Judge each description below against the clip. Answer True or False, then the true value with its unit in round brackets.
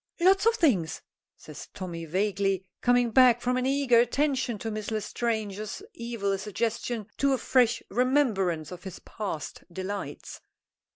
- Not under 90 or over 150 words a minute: True (135 wpm)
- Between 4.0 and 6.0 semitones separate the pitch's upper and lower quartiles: True (4.5 semitones)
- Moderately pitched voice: False (225 Hz)